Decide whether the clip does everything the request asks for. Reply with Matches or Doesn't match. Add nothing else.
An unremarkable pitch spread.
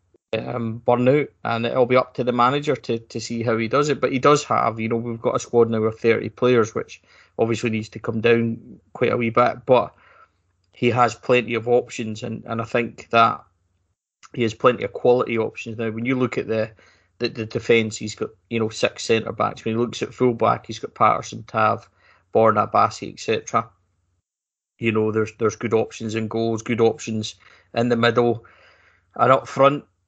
Doesn't match